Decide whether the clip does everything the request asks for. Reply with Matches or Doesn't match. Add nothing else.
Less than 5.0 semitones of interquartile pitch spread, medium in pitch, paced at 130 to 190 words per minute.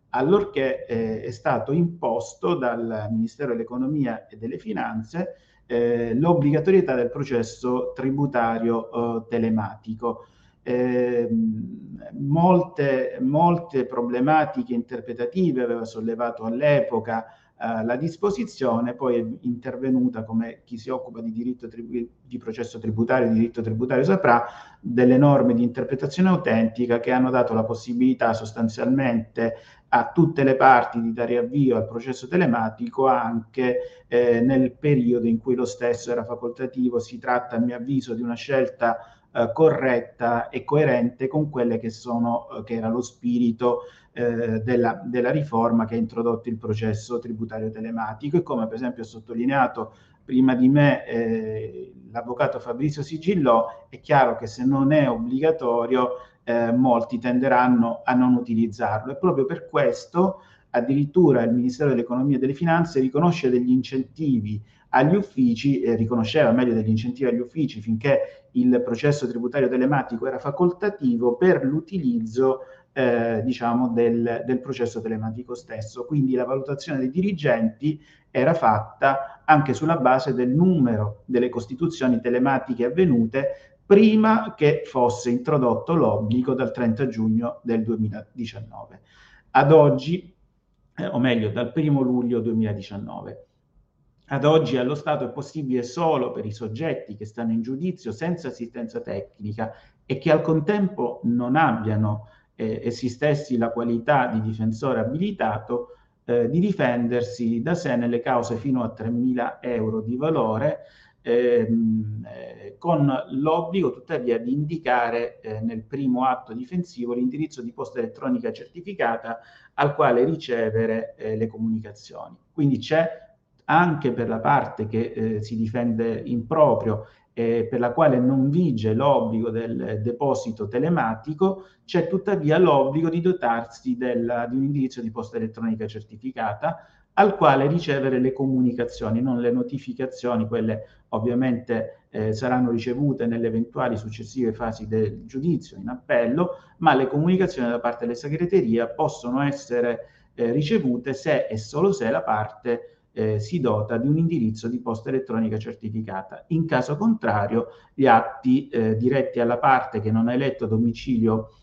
Doesn't match